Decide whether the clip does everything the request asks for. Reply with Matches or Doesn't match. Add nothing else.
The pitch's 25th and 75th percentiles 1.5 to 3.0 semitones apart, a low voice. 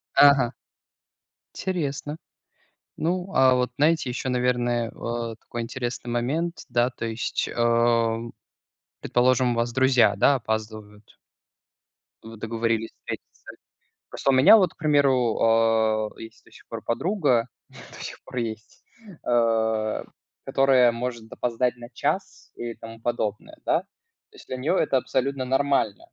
Matches